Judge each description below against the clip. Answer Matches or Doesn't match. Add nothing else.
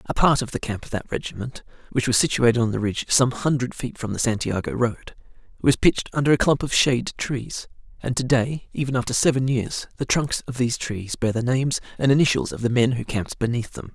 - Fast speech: Matches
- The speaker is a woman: Doesn't match